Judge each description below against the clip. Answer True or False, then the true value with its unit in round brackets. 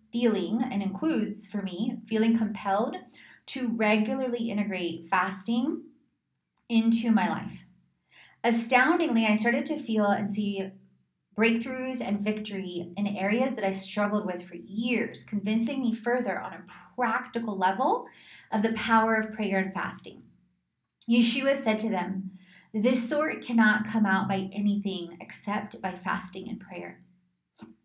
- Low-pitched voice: False (215 Hz)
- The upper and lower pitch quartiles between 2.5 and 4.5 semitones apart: True (3.5 semitones)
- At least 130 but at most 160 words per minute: True (135 wpm)